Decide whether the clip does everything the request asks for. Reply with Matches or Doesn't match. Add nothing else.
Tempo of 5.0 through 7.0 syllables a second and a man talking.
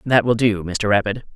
Matches